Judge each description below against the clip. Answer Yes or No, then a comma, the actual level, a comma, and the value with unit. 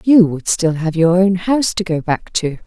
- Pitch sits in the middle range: Yes, medium, 180 Hz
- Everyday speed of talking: No, fast, 250 wpm